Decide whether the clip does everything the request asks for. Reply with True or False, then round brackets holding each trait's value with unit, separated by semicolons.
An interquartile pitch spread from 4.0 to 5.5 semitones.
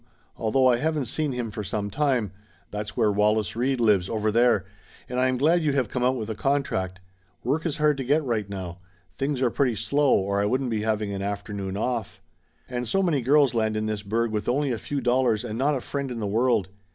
True (4.3 semitones)